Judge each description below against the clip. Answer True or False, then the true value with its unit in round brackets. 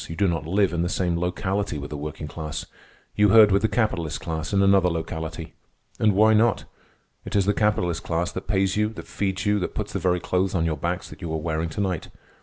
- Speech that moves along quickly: True (235 wpm)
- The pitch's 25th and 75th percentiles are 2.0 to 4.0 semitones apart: True (3.6 semitones)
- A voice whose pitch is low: True (90 Hz)